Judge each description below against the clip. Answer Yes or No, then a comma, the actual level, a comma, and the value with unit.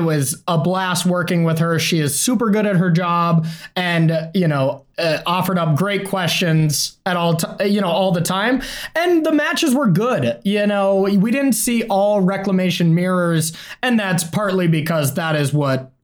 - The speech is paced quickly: No, average, 185 wpm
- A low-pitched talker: No, medium, 180 Hz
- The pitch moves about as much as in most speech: Yes, average, 3.8 semitones